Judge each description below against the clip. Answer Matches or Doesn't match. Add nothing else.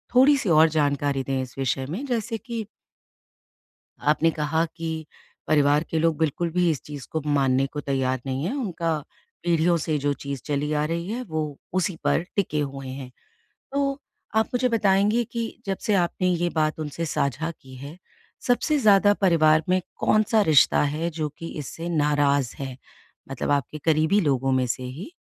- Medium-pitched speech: Matches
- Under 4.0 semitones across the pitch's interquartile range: Doesn't match